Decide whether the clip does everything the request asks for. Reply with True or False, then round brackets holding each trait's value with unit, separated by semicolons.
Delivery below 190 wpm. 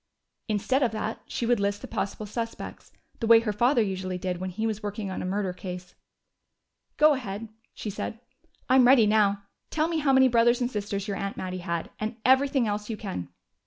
False (200 wpm)